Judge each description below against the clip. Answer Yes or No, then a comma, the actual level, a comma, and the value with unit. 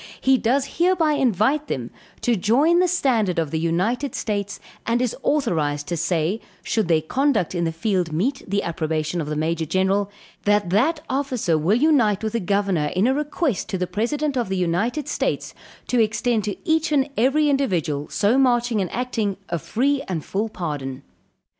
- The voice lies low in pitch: No, high, 210 Hz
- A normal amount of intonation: No, wide, 7.5 semitones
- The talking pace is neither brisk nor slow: Yes, average, 180 wpm